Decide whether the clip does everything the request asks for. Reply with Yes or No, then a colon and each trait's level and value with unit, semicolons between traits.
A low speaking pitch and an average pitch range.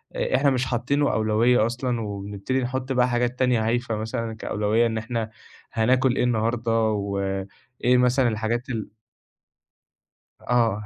No: low, 120 Hz; narrow, 2.3 semitones